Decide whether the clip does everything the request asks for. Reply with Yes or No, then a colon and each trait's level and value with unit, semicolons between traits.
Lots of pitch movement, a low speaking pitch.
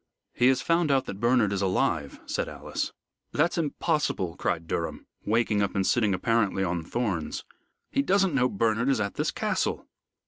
Yes: wide, 5.7 semitones; low, 115 Hz